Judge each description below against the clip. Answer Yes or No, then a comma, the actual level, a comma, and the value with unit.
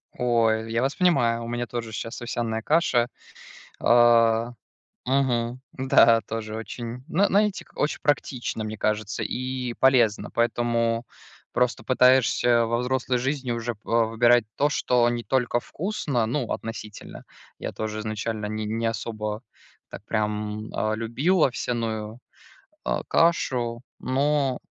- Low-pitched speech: Yes, low, 120 Hz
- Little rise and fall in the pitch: Yes, narrow, 2.3 semitones